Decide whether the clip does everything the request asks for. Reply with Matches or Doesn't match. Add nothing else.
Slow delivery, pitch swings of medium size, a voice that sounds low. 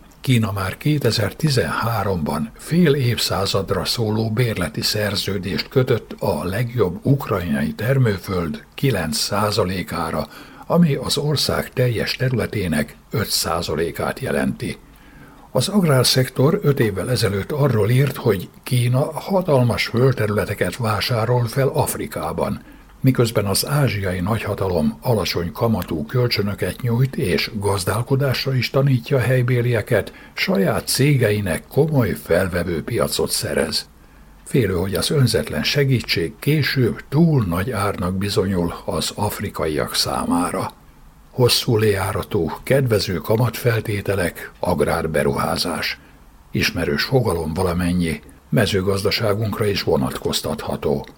Matches